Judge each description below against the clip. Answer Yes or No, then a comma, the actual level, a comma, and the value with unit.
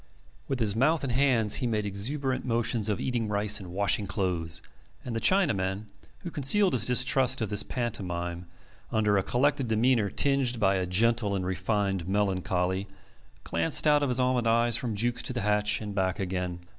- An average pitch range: Yes, average, 4.4 semitones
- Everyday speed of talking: Yes, average, 180 wpm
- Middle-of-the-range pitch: No, low, 110 Hz